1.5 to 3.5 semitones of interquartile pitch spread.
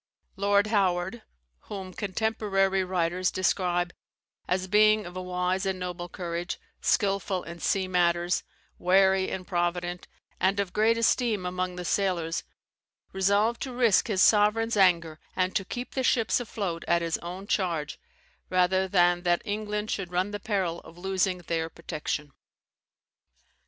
Yes: narrow, 2.5 semitones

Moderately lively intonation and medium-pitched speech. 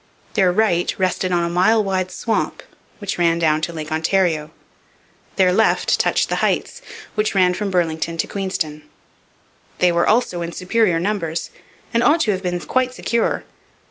Yes: average, 3.6 semitones; medium, 180 Hz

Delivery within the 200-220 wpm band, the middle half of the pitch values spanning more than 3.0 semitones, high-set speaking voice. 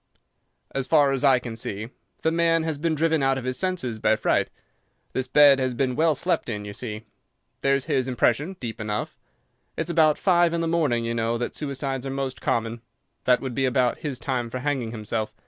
No: fast, 205 wpm; average, 4.2 semitones; low, 130 Hz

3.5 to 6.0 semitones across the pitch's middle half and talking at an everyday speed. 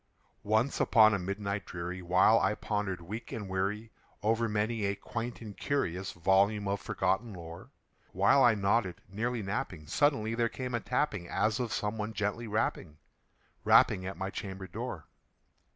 No: average, 3.0 semitones; average, 160 wpm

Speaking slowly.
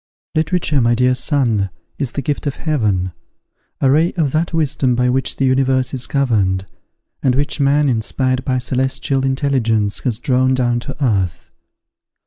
No: average, 160 wpm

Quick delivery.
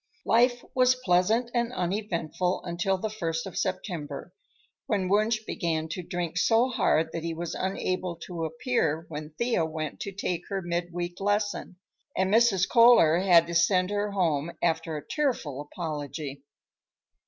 No: average, 155 wpm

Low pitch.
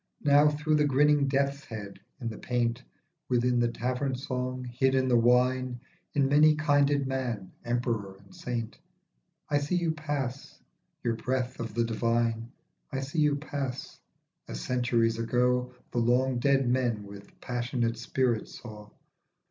Yes: low, 125 Hz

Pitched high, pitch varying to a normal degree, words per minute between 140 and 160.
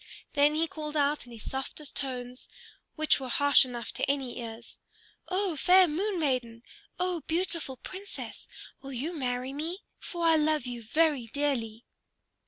Yes: very high, 285 Hz; average, 4.7 semitones; average, 155 wpm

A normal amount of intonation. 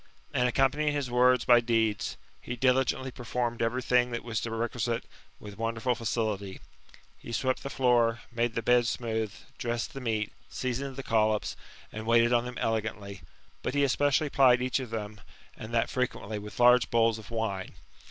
No: narrow, 2.1 semitones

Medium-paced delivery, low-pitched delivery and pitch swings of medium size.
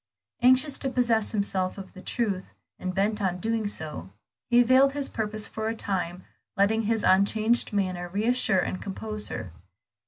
No: average, 160 wpm; high, 210 Hz; average, 3.4 semitones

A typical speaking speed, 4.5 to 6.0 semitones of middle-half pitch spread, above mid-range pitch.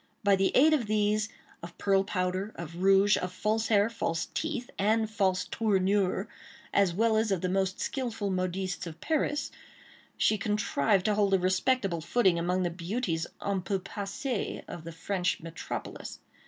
No: average, 165 wpm; average, 2.9 semitones; high, 195 Hz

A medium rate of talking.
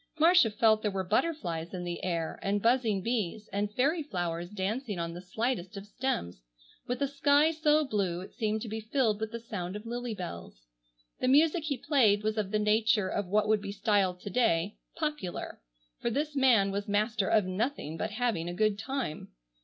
Yes: average, 195 wpm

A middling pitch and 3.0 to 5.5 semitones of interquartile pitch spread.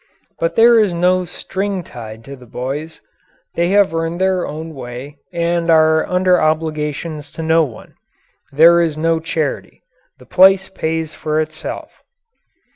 No: medium, 160 Hz; narrow, 2.6 semitones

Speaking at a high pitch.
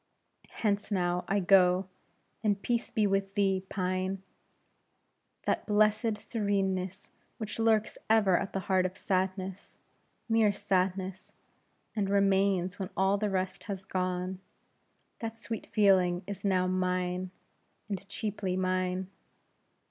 Yes: high, 195 Hz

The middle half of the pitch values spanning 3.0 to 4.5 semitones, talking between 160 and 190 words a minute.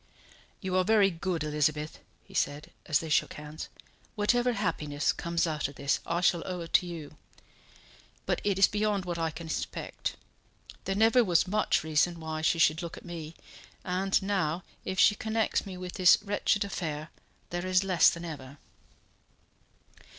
Yes: average, 3.7 semitones; average, 165 wpm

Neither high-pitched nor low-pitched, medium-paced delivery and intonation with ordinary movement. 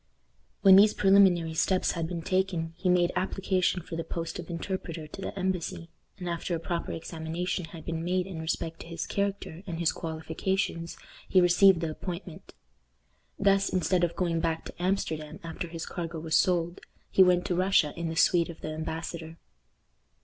No: medium, 170 Hz; average, 180 wpm; narrow, 2.1 semitones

